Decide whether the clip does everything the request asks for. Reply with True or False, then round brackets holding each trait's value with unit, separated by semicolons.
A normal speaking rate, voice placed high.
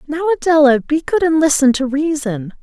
True (185 wpm; 290 Hz)